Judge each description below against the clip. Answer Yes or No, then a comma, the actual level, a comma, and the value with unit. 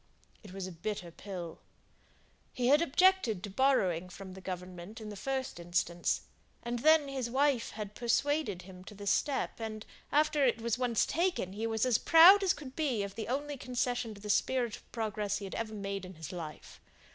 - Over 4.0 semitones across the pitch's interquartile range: Yes, wide, 5.5 semitones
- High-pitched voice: Yes, high, 220 Hz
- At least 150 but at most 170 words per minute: No, average, 190 wpm